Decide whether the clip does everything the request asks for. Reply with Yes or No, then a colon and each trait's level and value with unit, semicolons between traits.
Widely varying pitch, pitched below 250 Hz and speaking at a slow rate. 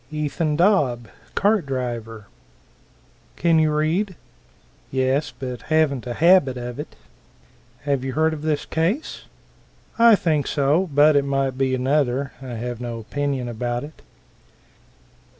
No: average, 3.9 semitones; medium, 140 Hz; slow, 130 wpm